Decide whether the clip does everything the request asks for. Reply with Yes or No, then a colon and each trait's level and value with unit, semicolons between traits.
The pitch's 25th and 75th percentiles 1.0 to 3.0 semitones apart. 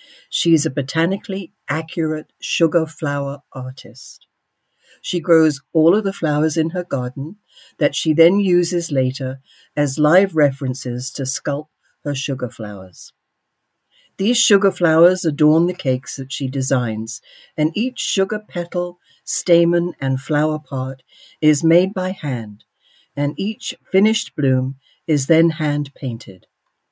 No: average, 4.5 semitones